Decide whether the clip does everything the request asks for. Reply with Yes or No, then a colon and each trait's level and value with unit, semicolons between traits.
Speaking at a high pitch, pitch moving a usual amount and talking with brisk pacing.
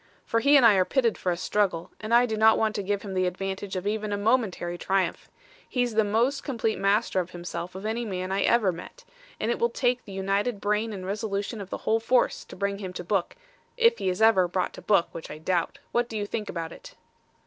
Yes: high, 205 Hz; average, 3.3 semitones; fast, 245 wpm